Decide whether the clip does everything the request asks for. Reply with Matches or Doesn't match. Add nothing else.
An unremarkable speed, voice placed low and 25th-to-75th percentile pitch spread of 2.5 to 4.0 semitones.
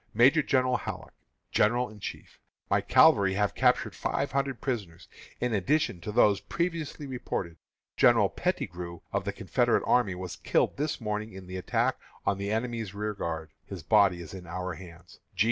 Doesn't match